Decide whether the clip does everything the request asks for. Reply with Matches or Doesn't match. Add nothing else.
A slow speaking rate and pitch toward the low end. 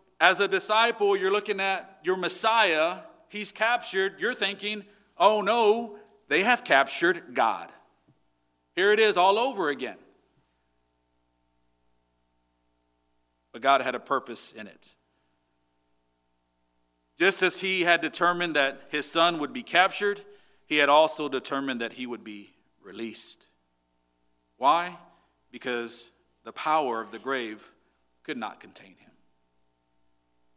Matches